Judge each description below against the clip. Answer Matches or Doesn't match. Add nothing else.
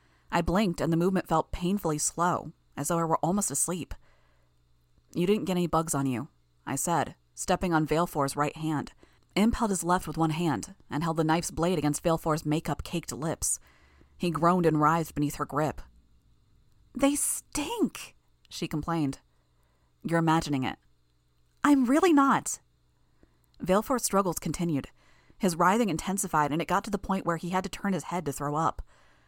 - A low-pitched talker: Doesn't match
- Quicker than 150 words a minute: Matches